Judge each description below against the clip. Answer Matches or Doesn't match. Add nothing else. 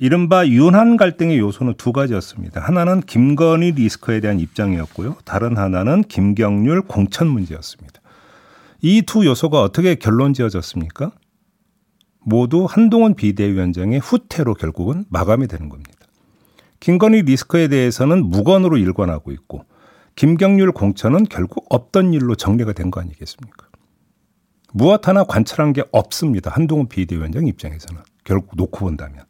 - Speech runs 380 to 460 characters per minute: Doesn't match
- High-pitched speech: Doesn't match